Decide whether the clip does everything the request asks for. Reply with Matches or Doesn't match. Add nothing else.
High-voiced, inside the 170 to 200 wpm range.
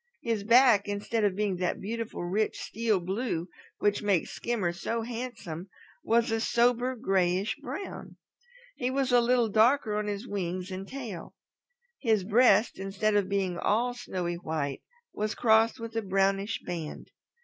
Doesn't match